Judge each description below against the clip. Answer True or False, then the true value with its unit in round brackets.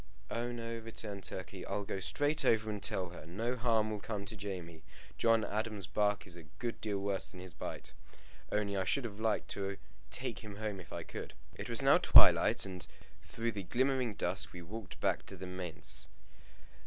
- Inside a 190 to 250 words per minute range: True (195 wpm)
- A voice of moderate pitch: False (105 Hz)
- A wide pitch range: False (3.3 semitones)